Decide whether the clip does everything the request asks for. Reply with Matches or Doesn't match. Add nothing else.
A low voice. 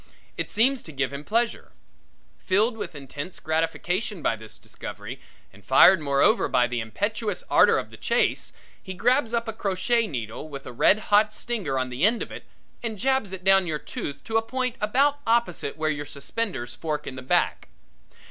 Doesn't match